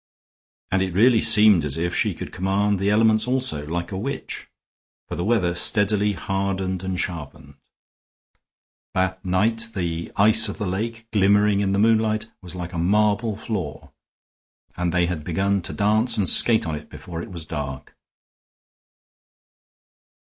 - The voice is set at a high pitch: No, very low, 95 Hz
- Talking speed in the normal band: Yes, average, 155 wpm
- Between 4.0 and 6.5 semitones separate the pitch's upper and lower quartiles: No, average, 3.5 semitones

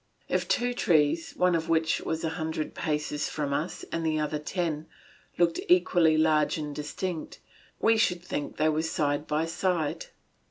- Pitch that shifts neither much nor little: No, narrow, 2.1 semitones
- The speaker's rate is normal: Yes, average, 165 wpm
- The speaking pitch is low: No, medium, 160 Hz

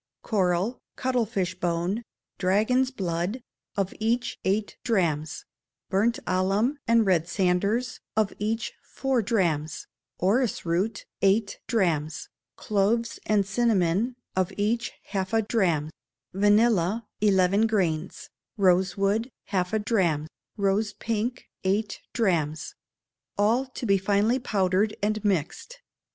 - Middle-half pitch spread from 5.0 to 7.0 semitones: No, average, 3.6 semitones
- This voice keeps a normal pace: No, slow, 110 wpm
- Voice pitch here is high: Yes, high, 200 Hz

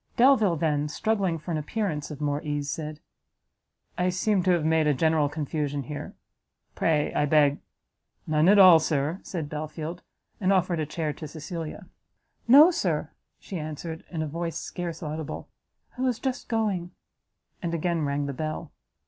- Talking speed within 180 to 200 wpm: No, average, 165 wpm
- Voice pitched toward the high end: No, medium, 160 Hz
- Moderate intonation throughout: Yes, average, 3.1 semitones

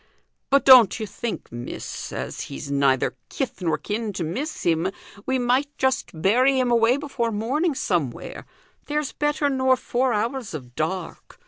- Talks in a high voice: Yes, high, 235 Hz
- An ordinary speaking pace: Yes, average, 155 wpm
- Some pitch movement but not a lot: No, wide, 6.6 semitones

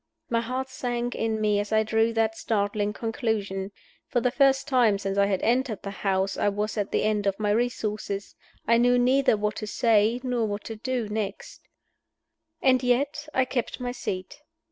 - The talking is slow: No, average, 190 wpm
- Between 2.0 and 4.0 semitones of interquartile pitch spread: Yes, average, 3.1 semitones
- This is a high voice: Yes, high, 220 Hz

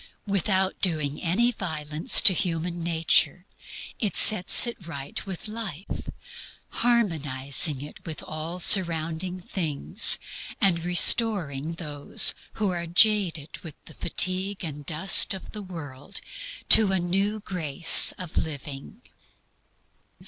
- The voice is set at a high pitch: No, medium, 175 Hz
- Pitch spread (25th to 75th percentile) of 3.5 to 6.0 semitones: Yes, average, 3.9 semitones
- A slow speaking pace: Yes, slow, 115 wpm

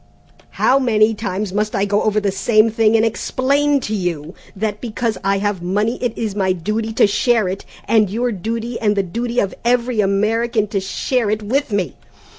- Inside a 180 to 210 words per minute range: Yes, average, 195 wpm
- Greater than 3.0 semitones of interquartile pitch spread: No, average, 2.7 semitones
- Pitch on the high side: Yes, high, 215 Hz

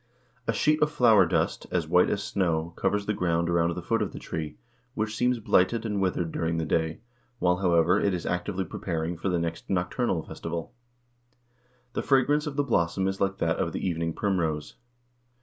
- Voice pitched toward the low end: Yes, very low, 90 Hz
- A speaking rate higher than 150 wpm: Yes, average, 190 wpm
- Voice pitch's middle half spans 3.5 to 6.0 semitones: Yes, average, 3.9 semitones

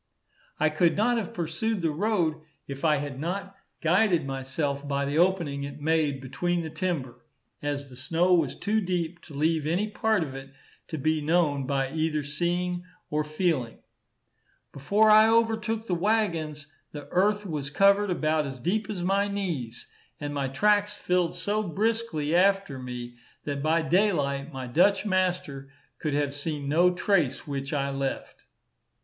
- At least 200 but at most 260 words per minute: No, average, 160 wpm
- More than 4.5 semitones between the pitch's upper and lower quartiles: Yes, average, 5.1 semitones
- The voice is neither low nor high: Yes, medium, 160 Hz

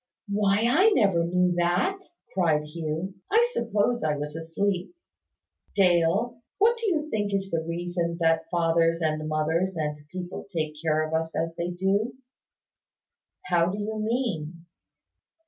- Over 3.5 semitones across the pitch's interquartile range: Yes, average, 4.0 semitones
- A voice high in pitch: No, medium, 175 Hz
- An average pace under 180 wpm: Yes, average, 145 wpm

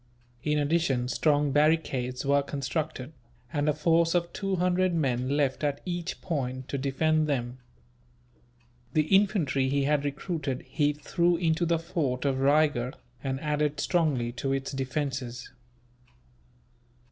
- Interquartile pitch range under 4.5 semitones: Yes, average, 3.3 semitones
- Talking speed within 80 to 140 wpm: Yes, slow, 135 wpm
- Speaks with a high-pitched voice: No, medium, 145 Hz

